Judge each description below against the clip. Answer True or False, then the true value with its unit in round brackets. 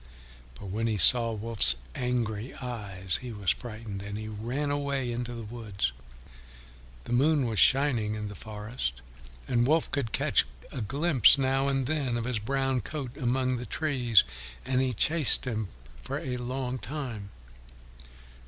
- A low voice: True (120 Hz)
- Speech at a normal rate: True (155 wpm)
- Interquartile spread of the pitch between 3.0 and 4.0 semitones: True (3.7 semitones)